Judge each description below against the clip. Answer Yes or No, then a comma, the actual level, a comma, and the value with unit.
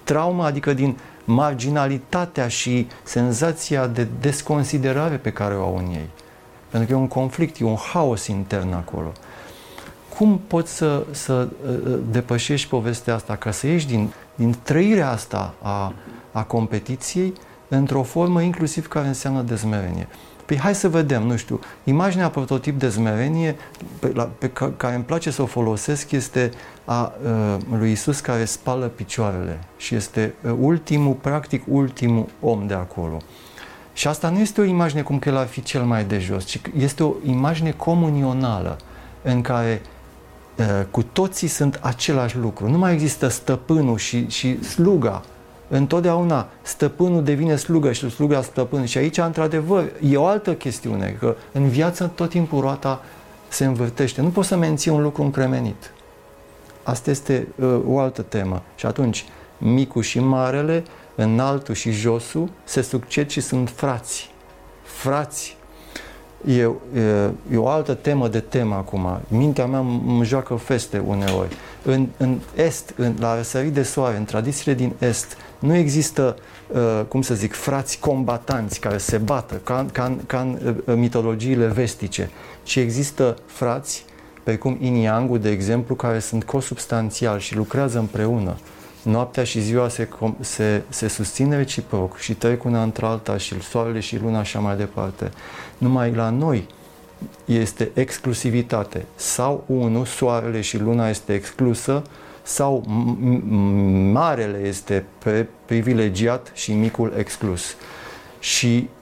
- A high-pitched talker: No, low, 125 Hz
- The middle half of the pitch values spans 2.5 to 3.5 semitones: No, average, 4.1 semitones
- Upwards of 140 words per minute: Yes, average, 150 wpm